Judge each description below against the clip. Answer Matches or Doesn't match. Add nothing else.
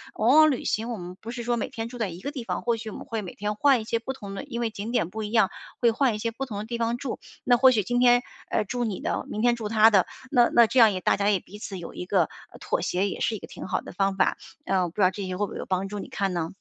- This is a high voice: Matches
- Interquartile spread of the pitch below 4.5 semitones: Matches